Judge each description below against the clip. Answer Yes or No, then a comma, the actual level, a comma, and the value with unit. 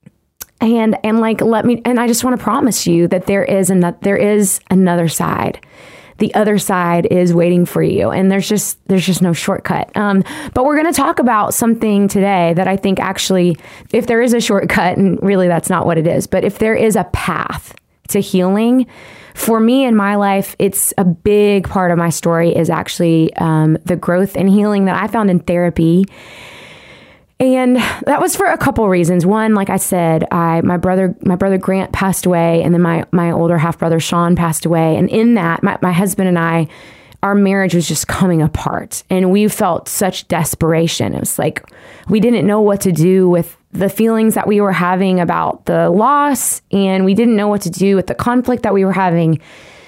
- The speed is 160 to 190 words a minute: No, fast, 205 wpm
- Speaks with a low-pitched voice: No, high, 190 Hz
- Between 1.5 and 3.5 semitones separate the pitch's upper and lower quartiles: Yes, average, 3.2 semitones